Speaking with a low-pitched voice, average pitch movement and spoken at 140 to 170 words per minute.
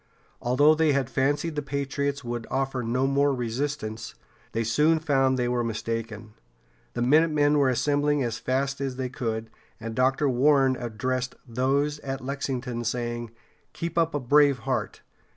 Yes: low, 130 Hz; average, 3.1 semitones; average, 150 wpm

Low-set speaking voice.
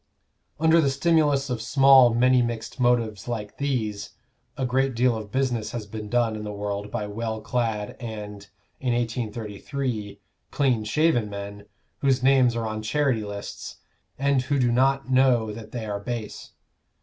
Yes: low, 120 Hz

